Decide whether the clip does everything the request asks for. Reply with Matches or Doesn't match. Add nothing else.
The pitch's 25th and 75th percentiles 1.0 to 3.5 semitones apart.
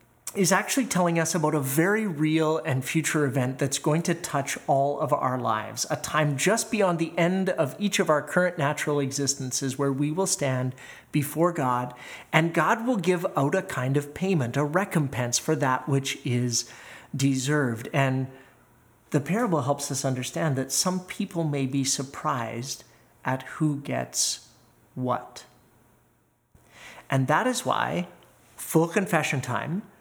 Doesn't match